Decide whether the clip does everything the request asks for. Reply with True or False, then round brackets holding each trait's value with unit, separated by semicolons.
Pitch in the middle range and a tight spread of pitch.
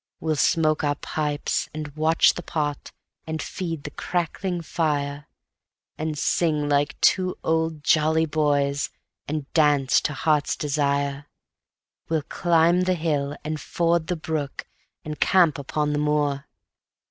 True (150 Hz; 1.9 semitones)